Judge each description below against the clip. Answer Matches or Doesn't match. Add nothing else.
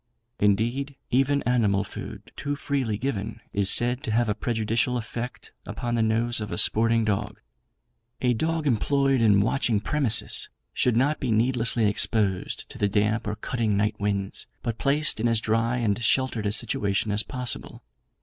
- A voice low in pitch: Matches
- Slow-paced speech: Doesn't match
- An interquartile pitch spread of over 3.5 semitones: Doesn't match